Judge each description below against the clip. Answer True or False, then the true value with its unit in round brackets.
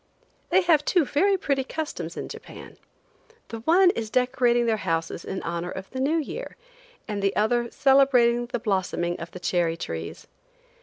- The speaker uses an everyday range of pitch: False (6.7 semitones)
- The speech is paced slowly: False (165 wpm)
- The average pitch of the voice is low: False (240 Hz)